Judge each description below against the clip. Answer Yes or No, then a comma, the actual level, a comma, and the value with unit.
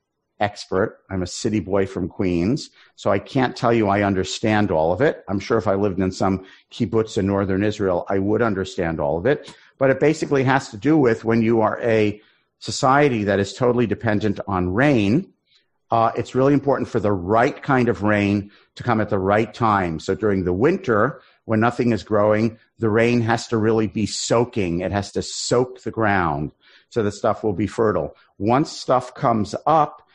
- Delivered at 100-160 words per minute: No, average, 195 wpm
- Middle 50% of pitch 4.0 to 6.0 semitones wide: No, average, 3.0 semitones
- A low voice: Yes, low, 110 Hz